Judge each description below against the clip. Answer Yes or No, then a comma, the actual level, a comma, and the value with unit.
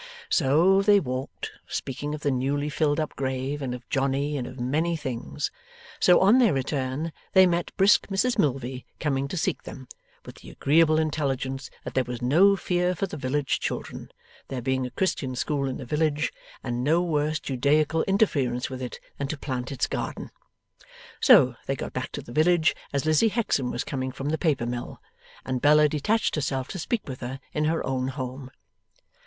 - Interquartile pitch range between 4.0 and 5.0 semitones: No, average, 3.5 semitones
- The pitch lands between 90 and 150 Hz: Yes, medium, 140 Hz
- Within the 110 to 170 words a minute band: No, average, 185 wpm